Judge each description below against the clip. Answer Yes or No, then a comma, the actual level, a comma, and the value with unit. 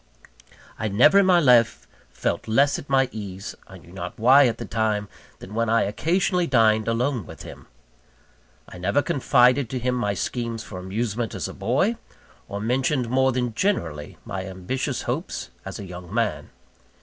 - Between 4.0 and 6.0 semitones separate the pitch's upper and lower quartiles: Yes, average, 4.7 semitones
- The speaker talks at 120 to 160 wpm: No, average, 175 wpm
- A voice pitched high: No, low, 115 Hz